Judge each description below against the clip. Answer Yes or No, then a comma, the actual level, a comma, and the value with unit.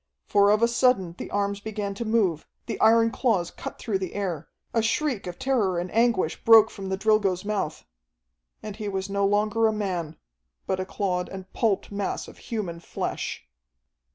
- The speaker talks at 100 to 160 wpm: No, average, 180 wpm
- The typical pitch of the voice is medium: No, high, 200 Hz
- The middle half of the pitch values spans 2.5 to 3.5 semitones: Yes, average, 2.9 semitones